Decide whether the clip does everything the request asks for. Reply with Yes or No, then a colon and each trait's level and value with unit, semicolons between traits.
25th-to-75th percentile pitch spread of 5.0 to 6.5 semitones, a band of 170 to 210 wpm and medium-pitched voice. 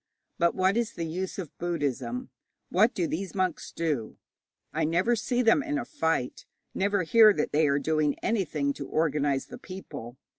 Yes: wide, 5.6 semitones; average, 175 wpm; medium, 170 Hz